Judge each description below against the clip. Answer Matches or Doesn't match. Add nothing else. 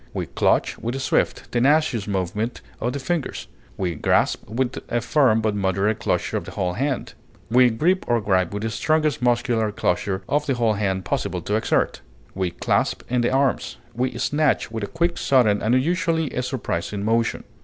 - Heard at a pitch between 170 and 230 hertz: Doesn't match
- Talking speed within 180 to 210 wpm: Matches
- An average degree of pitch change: Matches